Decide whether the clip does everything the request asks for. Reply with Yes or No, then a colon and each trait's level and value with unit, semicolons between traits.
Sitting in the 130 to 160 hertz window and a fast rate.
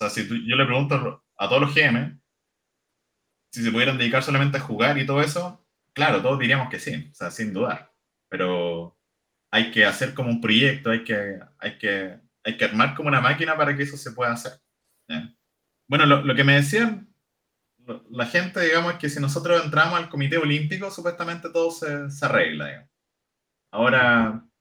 Yes: medium, 140 Hz; fast, 195 wpm